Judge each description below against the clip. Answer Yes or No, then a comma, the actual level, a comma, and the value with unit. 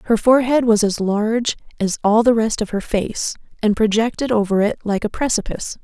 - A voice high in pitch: Yes, high, 220 Hz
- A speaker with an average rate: Yes, average, 195 wpm